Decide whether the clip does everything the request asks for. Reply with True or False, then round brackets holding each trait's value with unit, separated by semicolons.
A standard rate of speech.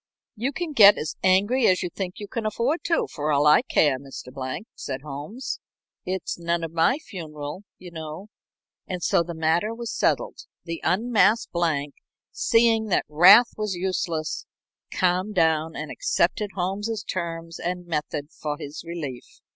True (160 wpm)